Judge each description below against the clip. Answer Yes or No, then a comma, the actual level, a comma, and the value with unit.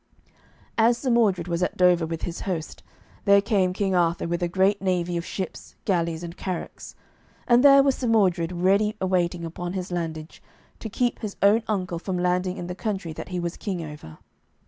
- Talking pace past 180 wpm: Yes, average, 190 wpm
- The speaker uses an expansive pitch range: No, average, 2.7 semitones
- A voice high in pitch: No, medium, 180 Hz